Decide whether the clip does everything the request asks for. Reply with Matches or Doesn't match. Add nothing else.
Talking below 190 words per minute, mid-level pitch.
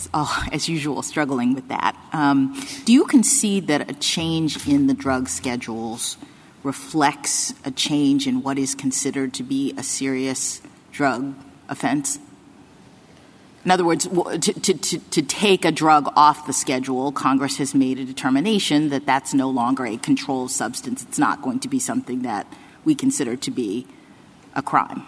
Matches